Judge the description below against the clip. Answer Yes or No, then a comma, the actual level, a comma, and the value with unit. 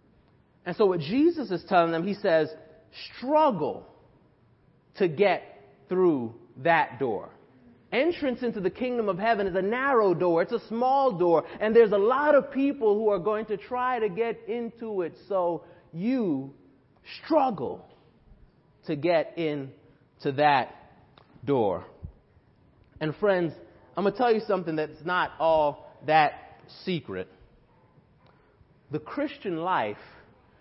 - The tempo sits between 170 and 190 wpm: No, slow, 135 wpm